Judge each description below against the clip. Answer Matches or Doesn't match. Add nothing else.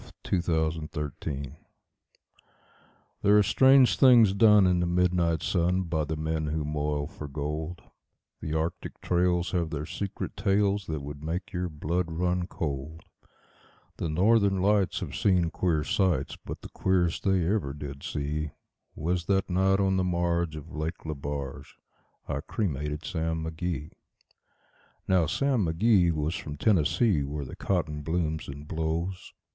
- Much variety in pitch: Doesn't match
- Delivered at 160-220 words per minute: Doesn't match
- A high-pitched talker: Doesn't match